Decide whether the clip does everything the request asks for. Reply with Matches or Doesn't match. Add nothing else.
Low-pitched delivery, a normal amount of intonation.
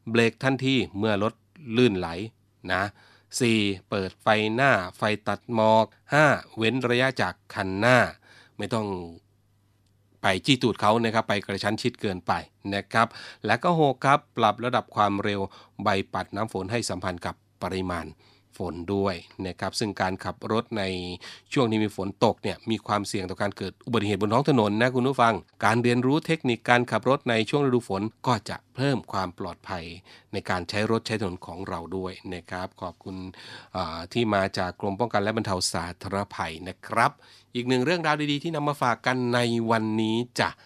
Matches